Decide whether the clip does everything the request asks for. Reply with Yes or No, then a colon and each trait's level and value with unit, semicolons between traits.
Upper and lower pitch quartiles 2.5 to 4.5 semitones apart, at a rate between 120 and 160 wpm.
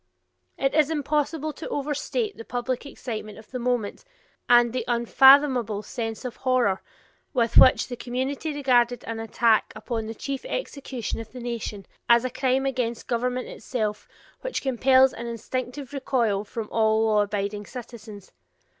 Yes: average, 3.0 semitones; average, 150 wpm